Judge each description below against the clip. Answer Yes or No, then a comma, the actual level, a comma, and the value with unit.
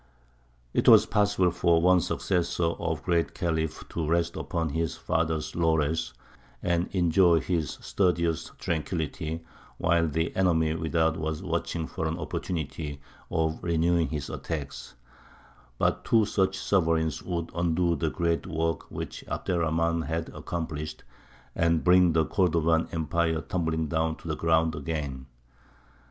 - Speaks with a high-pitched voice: No, very low, 80 Hz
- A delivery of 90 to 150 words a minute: Yes, average, 140 wpm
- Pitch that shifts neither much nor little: No, narrow, 1.4 semitones